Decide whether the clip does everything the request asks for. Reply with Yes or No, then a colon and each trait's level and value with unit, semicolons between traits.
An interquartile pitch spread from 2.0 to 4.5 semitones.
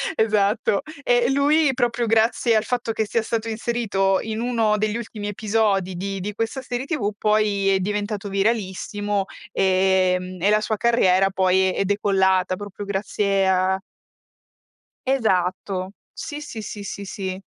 Yes: average, 2.8 semitones